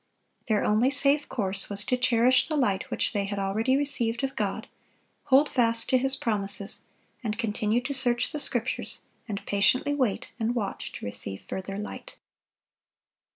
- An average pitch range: Yes, average, 4.2 semitones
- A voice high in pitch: Yes, high, 230 Hz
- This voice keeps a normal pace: Yes, average, 160 wpm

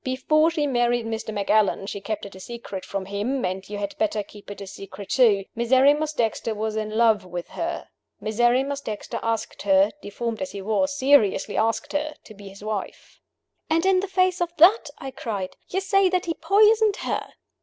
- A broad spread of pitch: Yes, wide, 6.4 semitones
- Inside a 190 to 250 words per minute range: Yes, average, 195 wpm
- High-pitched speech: Yes, high, 230 Hz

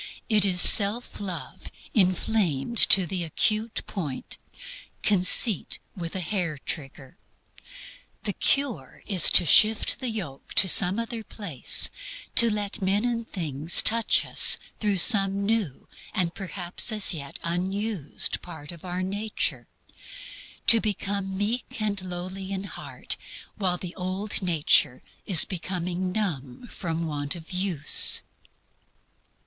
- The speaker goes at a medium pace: No, slow, 125 wpm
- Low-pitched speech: No, high, 190 Hz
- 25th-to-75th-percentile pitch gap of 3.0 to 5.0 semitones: Yes, average, 3.6 semitones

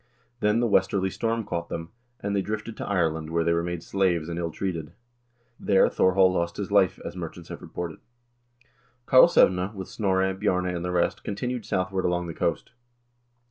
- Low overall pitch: Yes, very low, 95 Hz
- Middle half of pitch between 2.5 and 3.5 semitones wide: Yes, average, 2.8 semitones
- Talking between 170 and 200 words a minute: Yes, average, 180 wpm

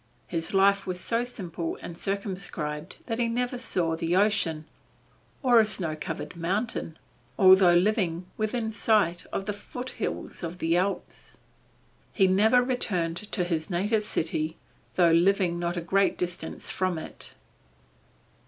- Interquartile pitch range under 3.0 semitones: No, average, 3.8 semitones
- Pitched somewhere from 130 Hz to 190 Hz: Yes, medium, 185 Hz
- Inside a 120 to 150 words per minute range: Yes, average, 140 wpm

